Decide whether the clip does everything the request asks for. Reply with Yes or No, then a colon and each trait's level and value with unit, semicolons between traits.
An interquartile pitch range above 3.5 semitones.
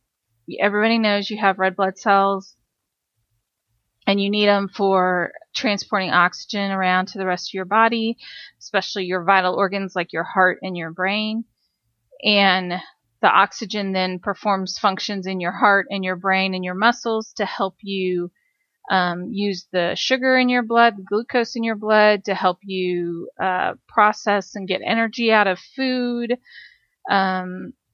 No: narrow, 2.5 semitones